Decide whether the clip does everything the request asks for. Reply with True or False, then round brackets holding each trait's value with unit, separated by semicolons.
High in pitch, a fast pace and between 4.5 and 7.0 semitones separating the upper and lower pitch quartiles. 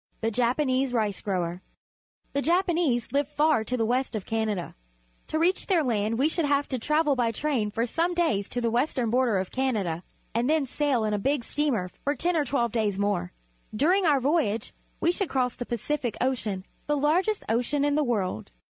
True (255 Hz; 210 wpm; 5.1 semitones)